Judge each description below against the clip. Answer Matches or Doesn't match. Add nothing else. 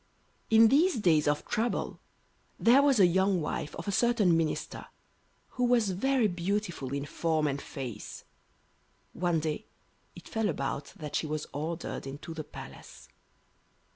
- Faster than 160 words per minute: Doesn't match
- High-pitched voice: Doesn't match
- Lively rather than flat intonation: Matches